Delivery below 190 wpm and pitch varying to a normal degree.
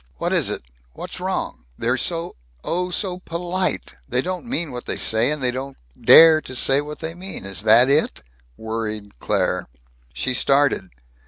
No: average, 170 wpm; wide, 7.0 semitones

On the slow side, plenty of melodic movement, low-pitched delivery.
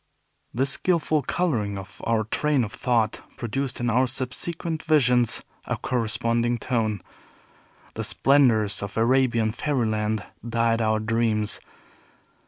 No: slow, 115 wpm; average, 3.4 semitones; low, 120 Hz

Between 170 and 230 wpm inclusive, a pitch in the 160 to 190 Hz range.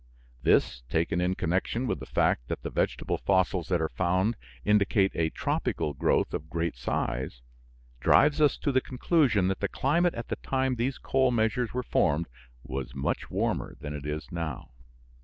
No: average, 175 wpm; very low, 95 Hz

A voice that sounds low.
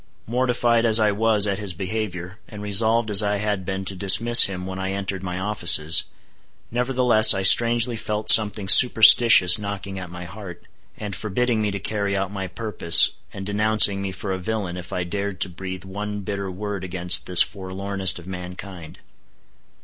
Yes: low, 100 Hz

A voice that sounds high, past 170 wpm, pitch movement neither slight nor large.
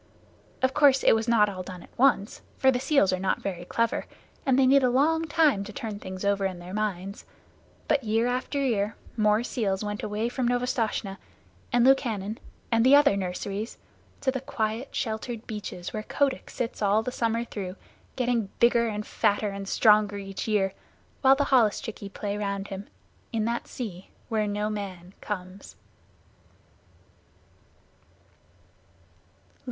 No: high, 215 Hz; average, 160 wpm; average, 3.8 semitones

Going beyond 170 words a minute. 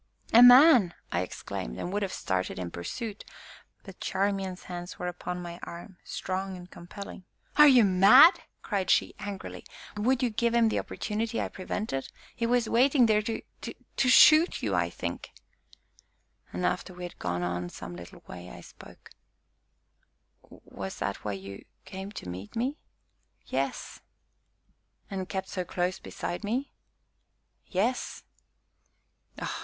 No: average, 145 wpm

